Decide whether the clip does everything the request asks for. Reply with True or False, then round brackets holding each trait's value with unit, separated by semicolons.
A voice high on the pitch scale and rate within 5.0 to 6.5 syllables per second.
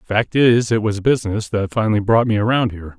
False (110 Hz; 5.8 syllables/s)